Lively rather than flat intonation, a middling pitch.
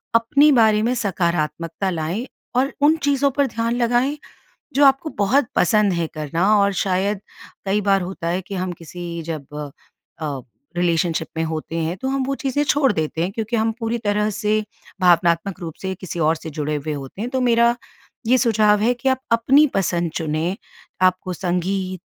No: wide, 5.7 semitones; high, 195 Hz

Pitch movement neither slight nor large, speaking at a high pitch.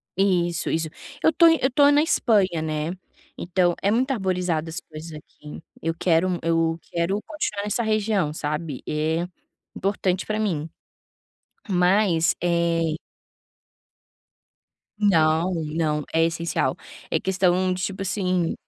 No: average, 3.3 semitones; medium, 175 Hz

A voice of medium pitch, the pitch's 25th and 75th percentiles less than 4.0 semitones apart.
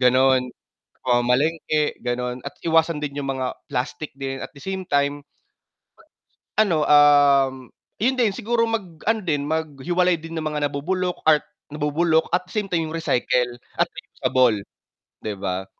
No: medium, 150 Hz; average, 4.4 semitones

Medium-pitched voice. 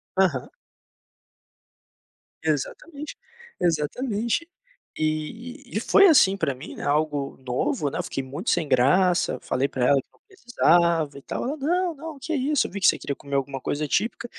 Yes: medium, 175 Hz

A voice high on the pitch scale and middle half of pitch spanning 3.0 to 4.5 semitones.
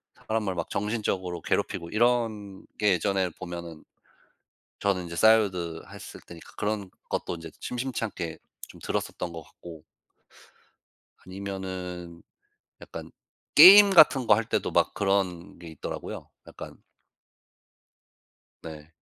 No: very low, 95 Hz; average, 3.9 semitones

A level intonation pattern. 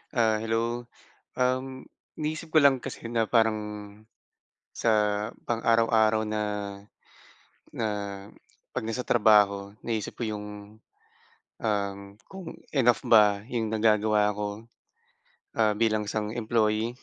Yes: narrow, 1.9 semitones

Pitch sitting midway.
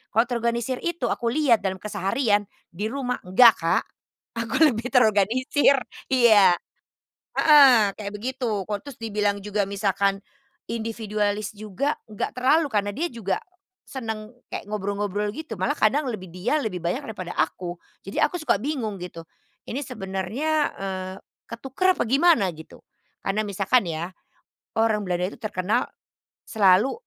No: high, 215 Hz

